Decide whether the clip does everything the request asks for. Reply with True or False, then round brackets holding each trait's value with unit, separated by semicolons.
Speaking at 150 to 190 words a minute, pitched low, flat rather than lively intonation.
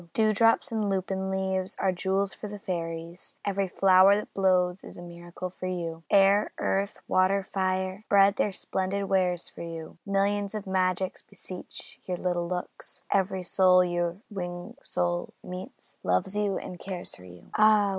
False (160 wpm; 190 Hz; 1.9 semitones)